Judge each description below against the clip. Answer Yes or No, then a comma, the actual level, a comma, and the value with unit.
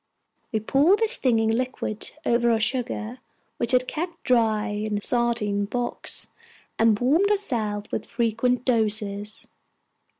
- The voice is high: Yes, high, 235 Hz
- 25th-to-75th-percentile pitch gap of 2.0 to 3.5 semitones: Yes, average, 2.8 semitones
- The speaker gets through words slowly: Yes, slow, 130 wpm